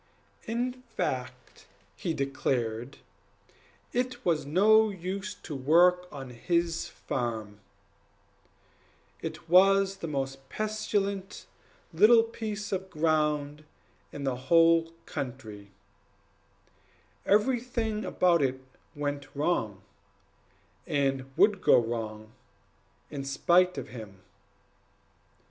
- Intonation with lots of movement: Yes, wide, 6.7 semitones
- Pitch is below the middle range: No, medium, 165 Hz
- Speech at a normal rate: No, slow, 95 wpm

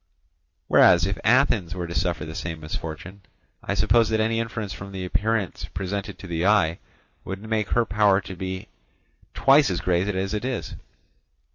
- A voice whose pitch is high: No, very low, 95 Hz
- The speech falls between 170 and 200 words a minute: Yes, average, 175 wpm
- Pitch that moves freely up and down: No, average, 3.8 semitones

